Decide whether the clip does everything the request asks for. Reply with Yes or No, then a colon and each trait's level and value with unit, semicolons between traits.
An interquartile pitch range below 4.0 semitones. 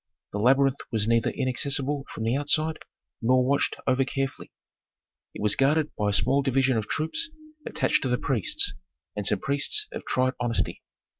Yes: average, 3.3 semitones